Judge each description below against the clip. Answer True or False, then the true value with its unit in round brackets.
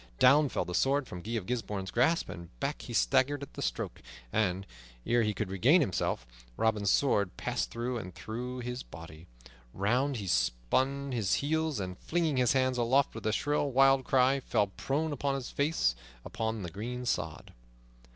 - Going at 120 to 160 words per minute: False (180 wpm)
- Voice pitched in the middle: False (120 Hz)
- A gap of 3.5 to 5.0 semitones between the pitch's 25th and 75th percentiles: False (5.6 semitones)